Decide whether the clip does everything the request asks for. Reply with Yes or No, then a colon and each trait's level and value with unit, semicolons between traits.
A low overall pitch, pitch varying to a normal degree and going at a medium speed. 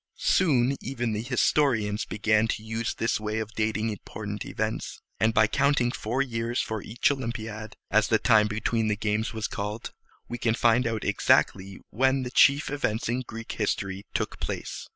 No: low, 110 Hz; narrow, 2.1 semitones; average, 175 wpm